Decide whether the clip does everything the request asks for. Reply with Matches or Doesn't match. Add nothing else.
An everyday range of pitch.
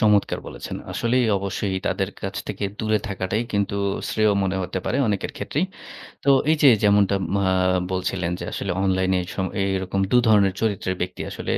Doesn't match